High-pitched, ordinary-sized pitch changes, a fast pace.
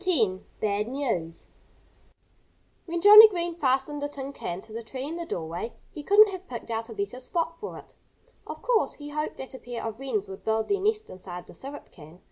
No: very high, 265 Hz; wide, 7.8 semitones; fast, 210 wpm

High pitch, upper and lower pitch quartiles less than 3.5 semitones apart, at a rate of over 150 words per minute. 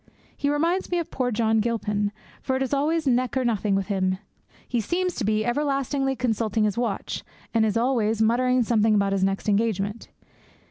No: high, 230 Hz; average, 4.1 semitones; average, 185 wpm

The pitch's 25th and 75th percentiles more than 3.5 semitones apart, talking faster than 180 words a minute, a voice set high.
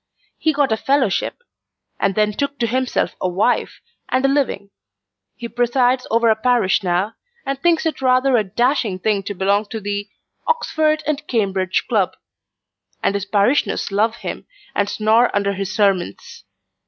No: average, 4.6 semitones; average, 160 wpm; high, 220 Hz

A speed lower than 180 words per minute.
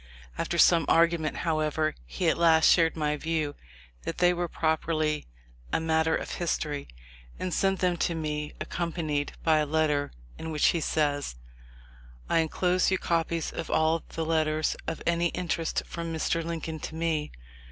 Yes: average, 165 wpm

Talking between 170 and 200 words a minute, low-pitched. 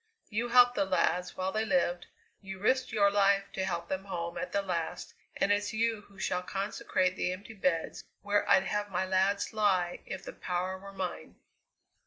No: average, 190 wpm; high, 195 Hz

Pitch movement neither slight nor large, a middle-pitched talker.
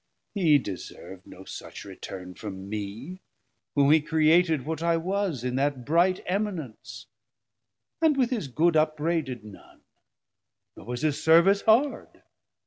No: wide, 6.0 semitones; medium, 155 Hz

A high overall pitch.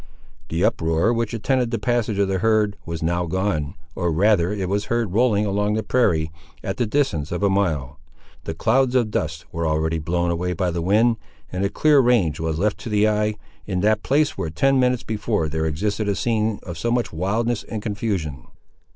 No: low, 100 Hz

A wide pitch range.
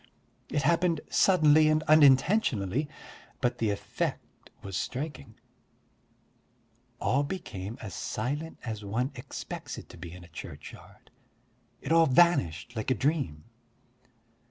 Yes: wide, 7.0 semitones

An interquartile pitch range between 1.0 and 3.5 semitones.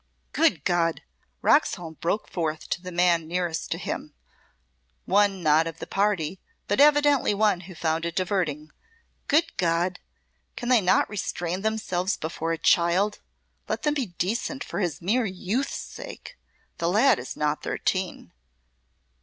No: average, 4.0 semitones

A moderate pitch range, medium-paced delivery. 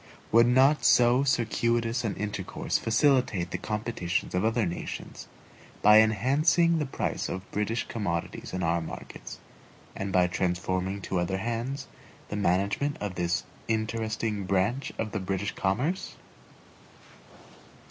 No: average, 4.2 semitones; slow, 125 wpm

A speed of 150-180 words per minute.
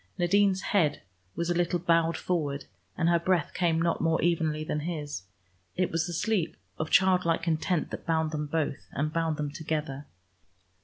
Yes: average, 170 wpm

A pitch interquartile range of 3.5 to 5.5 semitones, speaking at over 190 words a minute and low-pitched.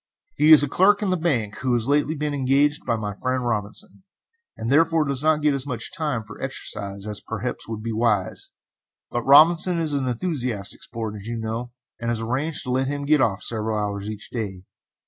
Yes: average, 5.1 semitones; fast, 205 wpm; low, 125 Hz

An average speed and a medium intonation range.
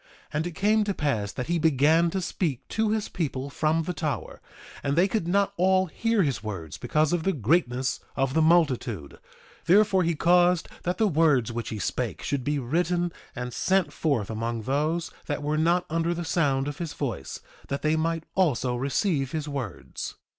Yes: average, 190 wpm; average, 4.6 semitones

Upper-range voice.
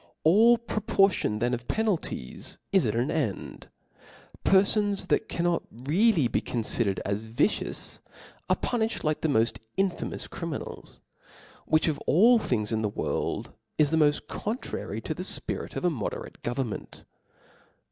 No: medium, 155 Hz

